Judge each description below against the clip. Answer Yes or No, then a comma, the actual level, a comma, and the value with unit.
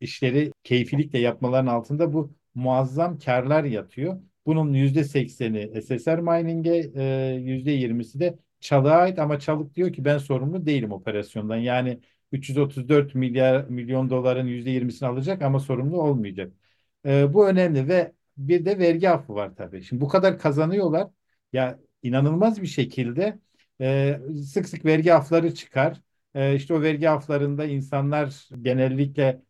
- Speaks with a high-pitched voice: No, medium, 140 Hz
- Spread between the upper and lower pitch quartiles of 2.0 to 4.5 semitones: Yes, average, 3.8 semitones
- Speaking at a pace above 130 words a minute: Yes, fast, 140 wpm